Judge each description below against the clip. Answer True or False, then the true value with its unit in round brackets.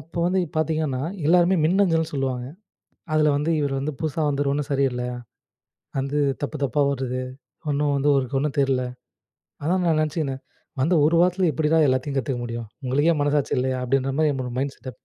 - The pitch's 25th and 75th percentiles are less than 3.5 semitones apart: True (2.9 semitones)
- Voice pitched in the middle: True (145 Hz)